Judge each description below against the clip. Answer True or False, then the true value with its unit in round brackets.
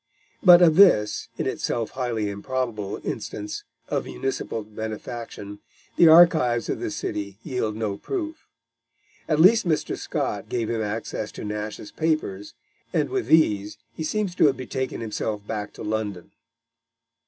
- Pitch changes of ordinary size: False (7.0 semitones)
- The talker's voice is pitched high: False (115 Hz)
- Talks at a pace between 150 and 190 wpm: False (140 wpm)